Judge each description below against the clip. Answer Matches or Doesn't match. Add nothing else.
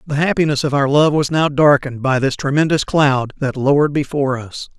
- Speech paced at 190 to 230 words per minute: Matches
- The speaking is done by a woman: Doesn't match